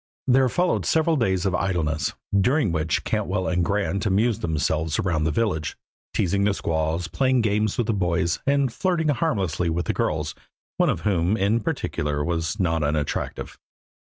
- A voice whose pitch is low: Yes, very low, 95 Hz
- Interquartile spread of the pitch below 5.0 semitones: No, wide, 5.6 semitones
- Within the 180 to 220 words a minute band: No, average, 160 wpm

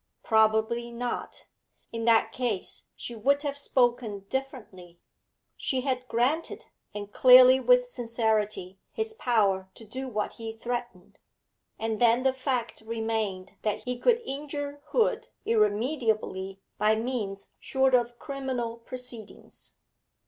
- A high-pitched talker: Yes, high, 235 Hz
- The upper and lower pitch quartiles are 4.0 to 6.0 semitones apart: No, average, 3.2 semitones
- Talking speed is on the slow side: Yes, slow, 120 wpm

